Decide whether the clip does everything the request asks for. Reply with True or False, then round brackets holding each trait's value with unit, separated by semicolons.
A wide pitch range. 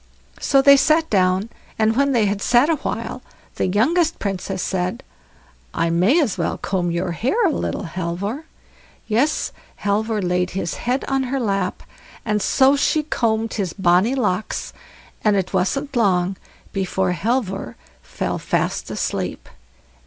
True (6.2 semitones)